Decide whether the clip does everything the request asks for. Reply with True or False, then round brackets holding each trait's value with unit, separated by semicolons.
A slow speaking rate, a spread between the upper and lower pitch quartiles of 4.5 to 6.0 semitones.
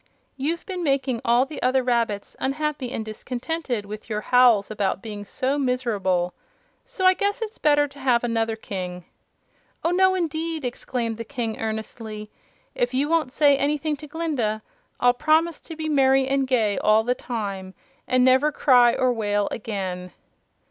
False (160 wpm; 5.2 semitones)